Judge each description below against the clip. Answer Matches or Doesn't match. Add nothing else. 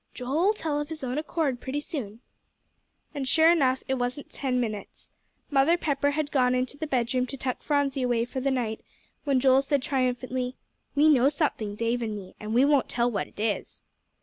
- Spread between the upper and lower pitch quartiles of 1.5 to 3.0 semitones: Matches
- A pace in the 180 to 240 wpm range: Matches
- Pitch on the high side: Matches